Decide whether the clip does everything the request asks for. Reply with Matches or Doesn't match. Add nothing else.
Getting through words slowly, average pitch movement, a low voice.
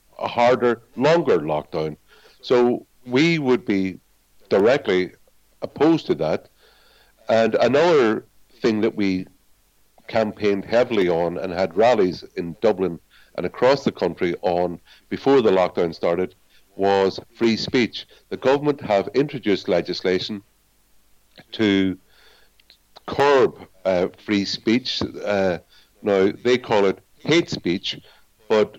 Matches